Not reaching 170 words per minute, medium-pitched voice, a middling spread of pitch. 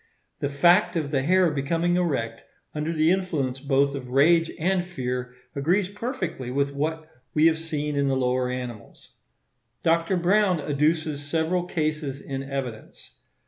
Yes: average, 145 wpm; medium, 150 Hz; average, 3.9 semitones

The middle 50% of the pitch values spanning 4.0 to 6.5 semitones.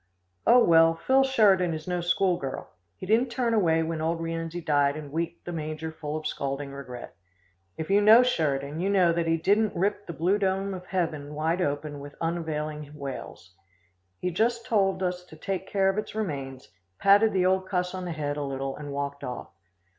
Yes: average, 4.4 semitones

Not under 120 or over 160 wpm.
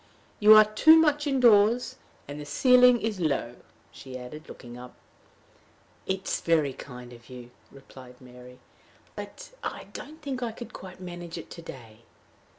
Yes: average, 155 wpm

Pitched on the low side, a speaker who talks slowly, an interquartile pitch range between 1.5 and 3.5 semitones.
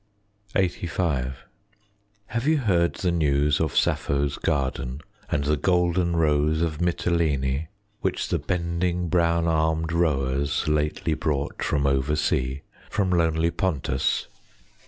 Yes: very low, 80 Hz; slow, 115 wpm; average, 3.2 semitones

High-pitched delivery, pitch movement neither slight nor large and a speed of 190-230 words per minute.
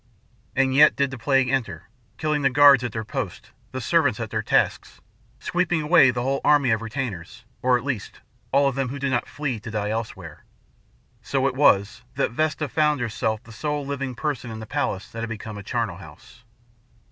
No: low, 125 Hz; average, 4.2 semitones; average, 200 wpm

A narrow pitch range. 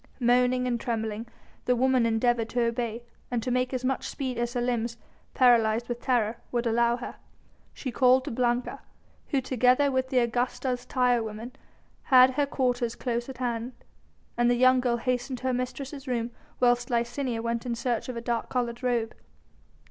Yes: narrow, 1.4 semitones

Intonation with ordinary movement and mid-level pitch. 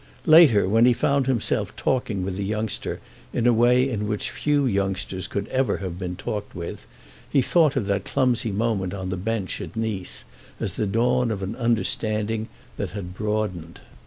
No: average, 3.8 semitones; low, 110 Hz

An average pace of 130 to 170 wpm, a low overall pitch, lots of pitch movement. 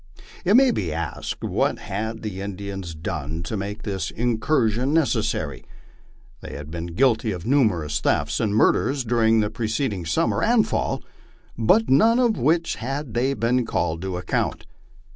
Yes: average, 160 wpm; low, 110 Hz; wide, 6.4 semitones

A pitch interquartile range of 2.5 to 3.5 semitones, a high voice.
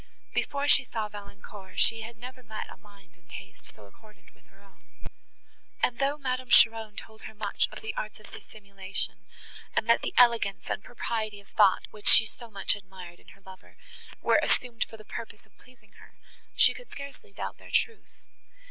Yes: average, 2.9 semitones; high, 215 Hz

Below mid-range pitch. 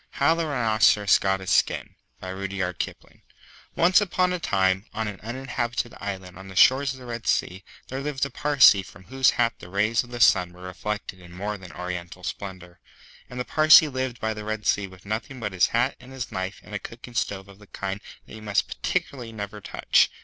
Yes: low, 105 Hz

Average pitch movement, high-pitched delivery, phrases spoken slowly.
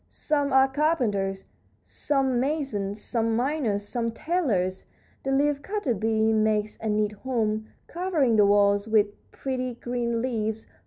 Yes: average, 4.3 semitones; high, 230 Hz; slow, 130 wpm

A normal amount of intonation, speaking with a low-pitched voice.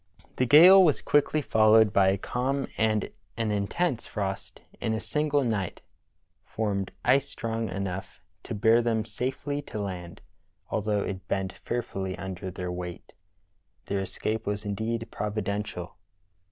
Yes: average, 3.5 semitones; low, 105 Hz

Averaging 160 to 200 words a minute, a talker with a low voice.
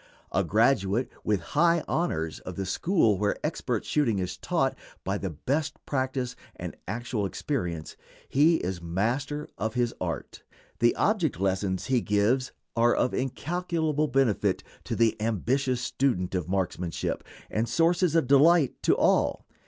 No: average, 145 wpm; low, 120 Hz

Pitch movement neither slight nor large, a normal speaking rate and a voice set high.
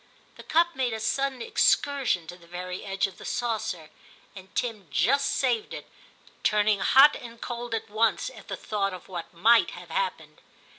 Yes: average, 4.8 semitones; average, 180 wpm; high, 220 Hz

